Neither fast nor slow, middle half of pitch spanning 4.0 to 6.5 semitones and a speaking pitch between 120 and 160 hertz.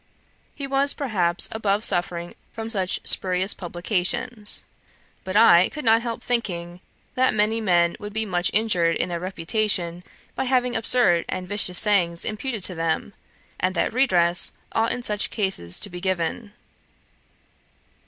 No: average, 145 wpm; average, 4.3 semitones; high, 200 Hz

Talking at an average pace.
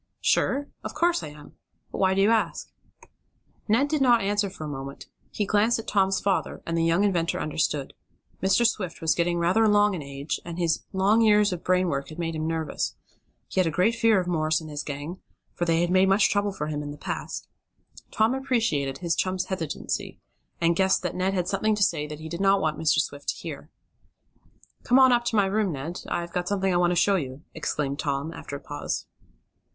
No: fast, 220 wpm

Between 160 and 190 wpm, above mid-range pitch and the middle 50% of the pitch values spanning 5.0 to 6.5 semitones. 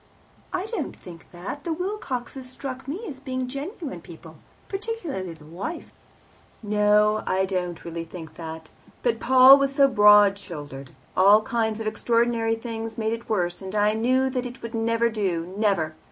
Yes: average, 170 wpm; high, 225 Hz; wide, 5.6 semitones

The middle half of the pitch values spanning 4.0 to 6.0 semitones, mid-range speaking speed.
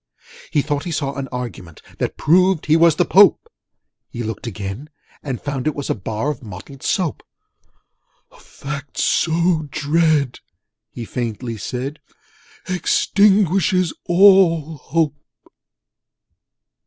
No: average, 5.1 semitones; slow, 120 wpm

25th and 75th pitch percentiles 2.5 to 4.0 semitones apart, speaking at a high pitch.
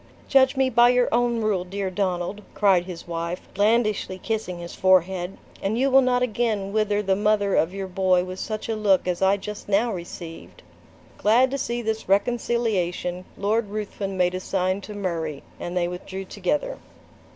Yes: average, 3.3 semitones; high, 200 Hz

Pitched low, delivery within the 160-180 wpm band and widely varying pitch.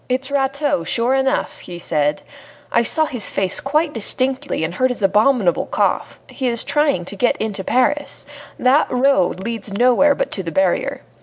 No: high, 245 Hz; average, 175 wpm; wide, 5.8 semitones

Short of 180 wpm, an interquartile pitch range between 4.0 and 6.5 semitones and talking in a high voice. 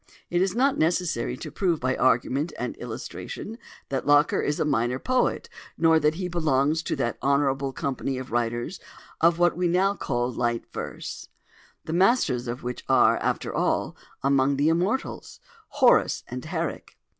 No: average, 155 wpm; average, 5.2 semitones; medium, 150 Hz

